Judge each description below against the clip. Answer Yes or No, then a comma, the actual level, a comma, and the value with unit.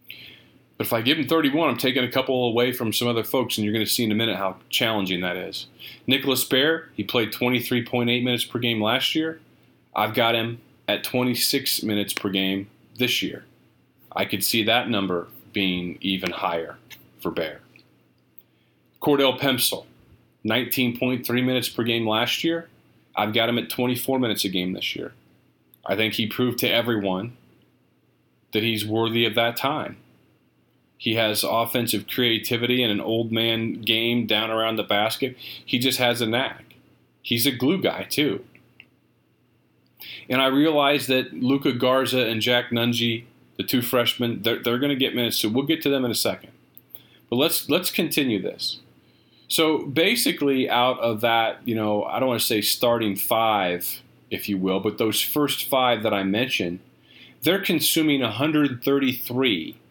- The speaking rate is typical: Yes, average, 165 wpm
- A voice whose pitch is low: Yes, low, 120 Hz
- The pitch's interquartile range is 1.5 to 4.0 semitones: Yes, average, 3.0 semitones